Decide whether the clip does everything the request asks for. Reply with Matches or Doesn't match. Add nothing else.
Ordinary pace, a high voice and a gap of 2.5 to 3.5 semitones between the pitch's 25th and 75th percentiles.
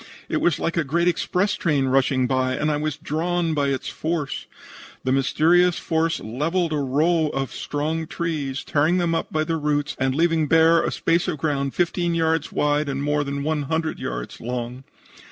Doesn't match